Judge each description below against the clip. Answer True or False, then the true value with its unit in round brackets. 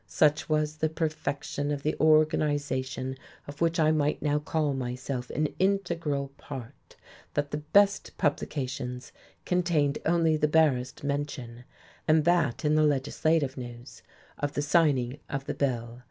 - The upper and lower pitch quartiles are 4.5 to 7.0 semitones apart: False (2.9 semitones)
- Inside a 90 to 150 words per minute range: True (140 wpm)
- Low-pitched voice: False (145 Hz)